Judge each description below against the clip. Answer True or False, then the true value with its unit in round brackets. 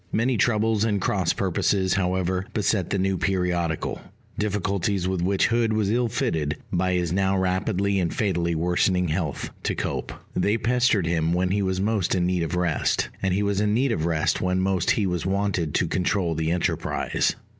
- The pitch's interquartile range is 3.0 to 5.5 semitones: False (2.5 semitones)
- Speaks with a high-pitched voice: False (95 Hz)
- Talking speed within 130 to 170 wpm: False (185 wpm)